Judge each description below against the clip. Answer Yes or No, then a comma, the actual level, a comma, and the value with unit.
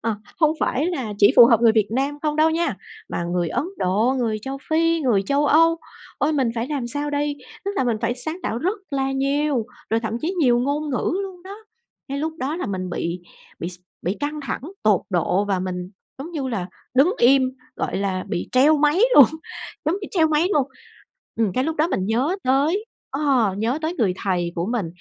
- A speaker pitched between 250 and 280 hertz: Yes, very high, 265 Hz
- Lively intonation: Yes, wide, 5.9 semitones